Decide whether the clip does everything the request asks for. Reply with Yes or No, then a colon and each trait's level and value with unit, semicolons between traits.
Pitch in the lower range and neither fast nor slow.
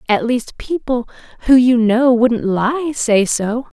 No: high, 240 Hz; average, 160 wpm